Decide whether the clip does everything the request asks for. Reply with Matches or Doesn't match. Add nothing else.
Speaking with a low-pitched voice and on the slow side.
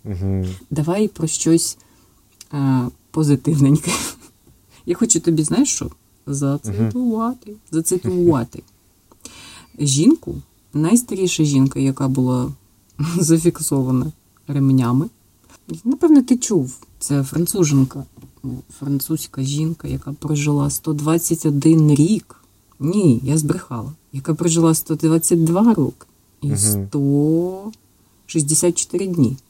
Doesn't match